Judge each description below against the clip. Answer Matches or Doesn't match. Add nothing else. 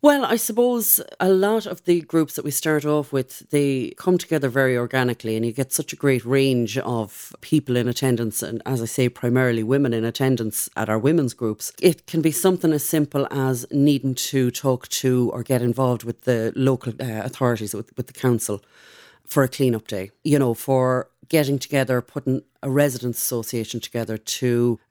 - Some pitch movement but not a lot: Matches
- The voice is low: Matches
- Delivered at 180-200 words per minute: Matches